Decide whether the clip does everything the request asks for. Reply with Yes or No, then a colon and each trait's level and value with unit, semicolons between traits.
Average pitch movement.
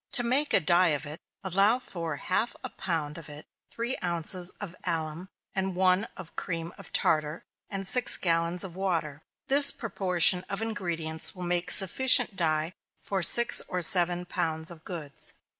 Yes: average, 3.1 semitones